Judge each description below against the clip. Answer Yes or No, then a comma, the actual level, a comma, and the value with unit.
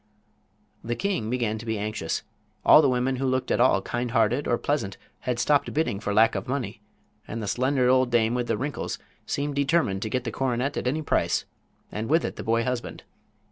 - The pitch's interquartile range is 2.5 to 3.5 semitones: Yes, average, 3.1 semitones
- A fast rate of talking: Yes, fast, 210 wpm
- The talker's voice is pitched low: Yes, low, 125 Hz